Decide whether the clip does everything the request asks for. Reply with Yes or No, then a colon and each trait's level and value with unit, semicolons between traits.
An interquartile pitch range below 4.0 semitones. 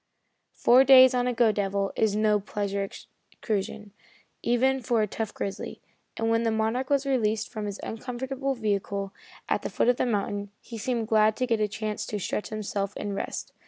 Yes: average, 3.0 semitones